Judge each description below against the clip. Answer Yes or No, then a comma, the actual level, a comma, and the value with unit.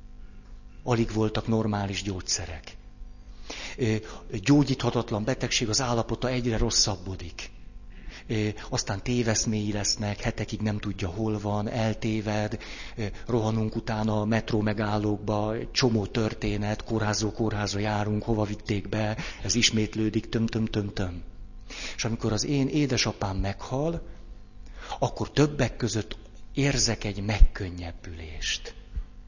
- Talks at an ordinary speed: No, slow, 95 wpm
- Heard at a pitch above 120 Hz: No, low, 110 Hz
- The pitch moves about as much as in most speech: No, narrow, 1.9 semitones